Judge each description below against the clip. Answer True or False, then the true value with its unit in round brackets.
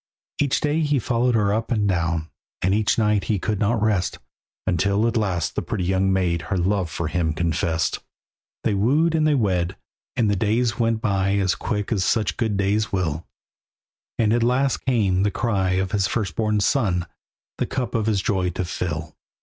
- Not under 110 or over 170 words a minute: False (190 wpm)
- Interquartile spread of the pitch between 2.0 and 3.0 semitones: False (3.7 semitones)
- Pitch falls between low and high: False (100 Hz)